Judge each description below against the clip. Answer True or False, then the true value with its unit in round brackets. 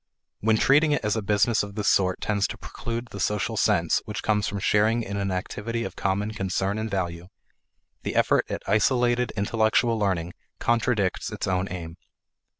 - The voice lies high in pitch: False (105 Hz)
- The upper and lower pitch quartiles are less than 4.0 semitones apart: True (2.7 semitones)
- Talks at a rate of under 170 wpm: False (175 wpm)